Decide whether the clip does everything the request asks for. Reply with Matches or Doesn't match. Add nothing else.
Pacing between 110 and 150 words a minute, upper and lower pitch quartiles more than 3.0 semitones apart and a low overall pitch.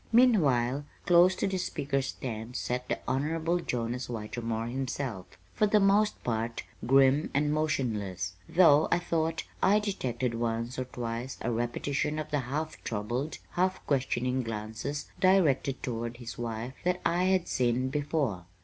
Matches